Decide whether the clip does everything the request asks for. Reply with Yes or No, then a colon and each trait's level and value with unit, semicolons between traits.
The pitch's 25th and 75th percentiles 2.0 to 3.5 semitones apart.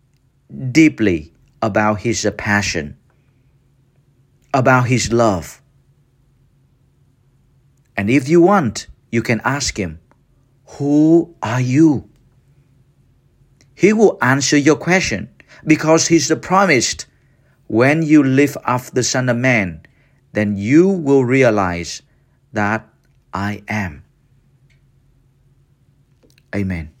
Yes: average, 3.2 semitones